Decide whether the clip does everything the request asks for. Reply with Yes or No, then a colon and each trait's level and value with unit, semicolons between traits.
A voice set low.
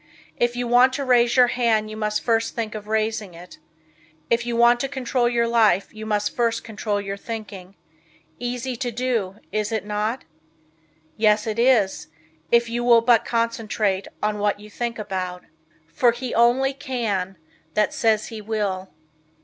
No: high, 225 Hz